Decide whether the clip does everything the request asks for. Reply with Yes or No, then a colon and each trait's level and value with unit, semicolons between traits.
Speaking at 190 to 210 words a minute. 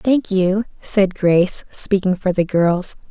No: average, 155 wpm